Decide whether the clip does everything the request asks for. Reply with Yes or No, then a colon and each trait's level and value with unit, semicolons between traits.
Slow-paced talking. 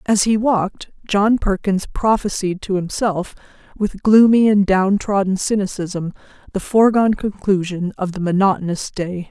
Yes: slow, 130 wpm